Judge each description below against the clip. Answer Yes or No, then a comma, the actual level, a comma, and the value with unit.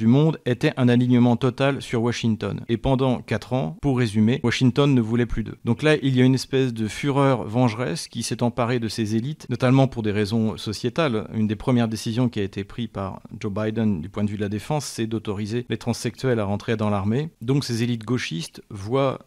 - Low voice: Yes, low, 120 Hz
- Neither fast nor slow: No, fast, 225 wpm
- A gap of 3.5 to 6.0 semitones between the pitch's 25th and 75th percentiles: No, average, 2.9 semitones